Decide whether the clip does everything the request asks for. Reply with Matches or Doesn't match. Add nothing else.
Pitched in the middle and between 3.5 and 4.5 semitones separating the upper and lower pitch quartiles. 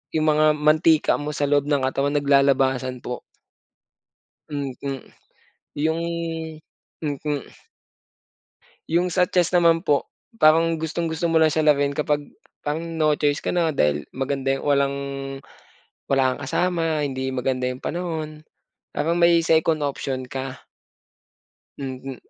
Doesn't match